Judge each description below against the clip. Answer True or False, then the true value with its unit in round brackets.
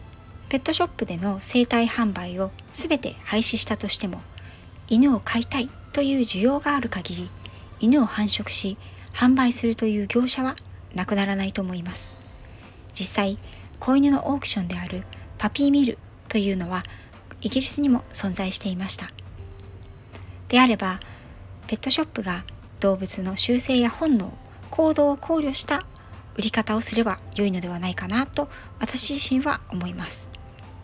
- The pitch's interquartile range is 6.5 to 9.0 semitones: True (6.8 semitones)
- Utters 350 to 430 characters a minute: False (305 characters per minute)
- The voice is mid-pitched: False (215 Hz)